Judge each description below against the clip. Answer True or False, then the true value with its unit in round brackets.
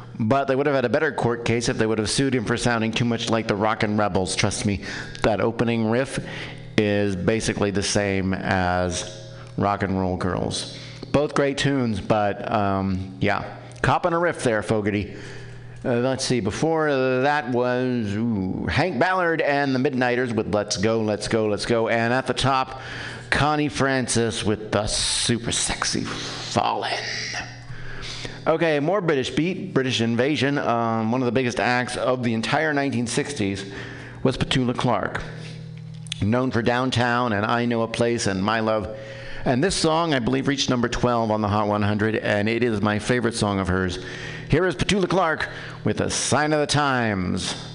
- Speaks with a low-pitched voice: True (120 Hz)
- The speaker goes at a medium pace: True (175 wpm)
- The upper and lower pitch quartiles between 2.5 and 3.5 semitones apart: False (4.1 semitones)